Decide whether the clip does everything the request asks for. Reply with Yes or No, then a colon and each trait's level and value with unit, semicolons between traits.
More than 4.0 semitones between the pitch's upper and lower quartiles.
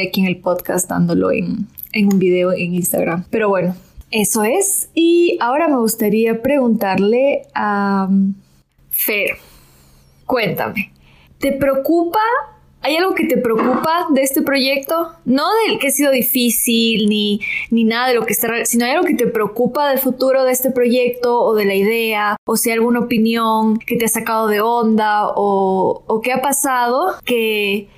Yes: average, 4.4 semitones